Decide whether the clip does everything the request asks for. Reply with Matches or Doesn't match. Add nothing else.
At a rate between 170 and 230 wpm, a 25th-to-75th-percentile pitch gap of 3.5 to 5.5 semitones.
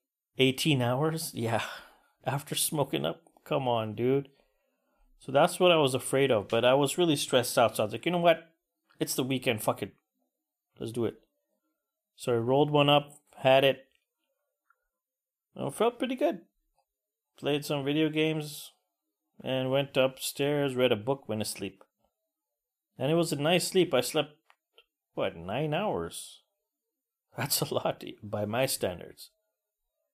Doesn't match